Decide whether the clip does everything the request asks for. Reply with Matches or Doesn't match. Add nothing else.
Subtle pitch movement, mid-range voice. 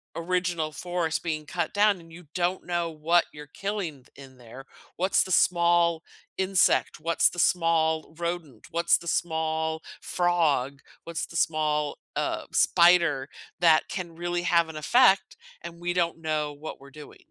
Matches